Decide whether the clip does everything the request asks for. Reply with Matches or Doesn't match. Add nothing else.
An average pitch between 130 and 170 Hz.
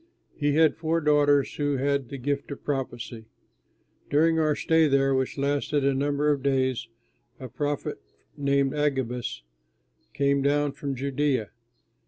Matches